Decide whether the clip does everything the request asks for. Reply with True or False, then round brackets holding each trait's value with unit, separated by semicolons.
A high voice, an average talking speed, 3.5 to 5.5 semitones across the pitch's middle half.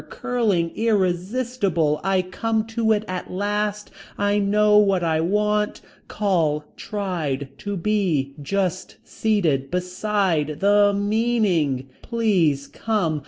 False (200 Hz; 110 wpm; 4.0 semitones)